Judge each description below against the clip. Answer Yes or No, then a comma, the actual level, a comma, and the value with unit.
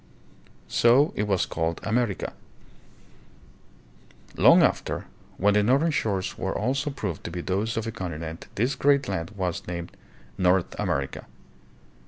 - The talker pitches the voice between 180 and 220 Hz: No, low, 100 Hz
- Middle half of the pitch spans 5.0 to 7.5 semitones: Yes, average, 5.3 semitones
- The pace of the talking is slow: Yes, slow, 130 wpm